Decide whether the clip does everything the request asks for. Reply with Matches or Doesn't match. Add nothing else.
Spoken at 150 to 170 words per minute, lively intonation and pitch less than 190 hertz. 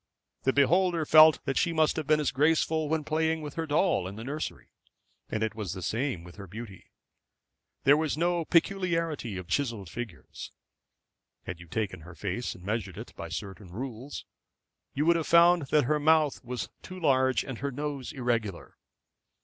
Doesn't match